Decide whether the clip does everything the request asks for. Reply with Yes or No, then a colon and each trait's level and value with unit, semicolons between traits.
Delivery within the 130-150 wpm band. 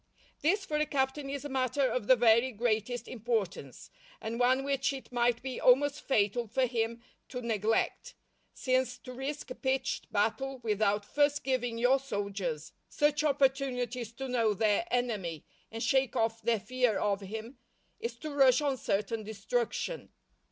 No: average, 160 wpm